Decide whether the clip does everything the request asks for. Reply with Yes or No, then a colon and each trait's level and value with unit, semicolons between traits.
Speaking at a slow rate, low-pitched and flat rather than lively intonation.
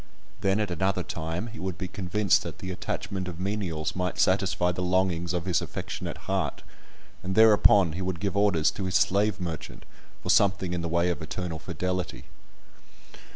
No: average, 175 wpm; very low, 90 Hz; narrow, 2.0 semitones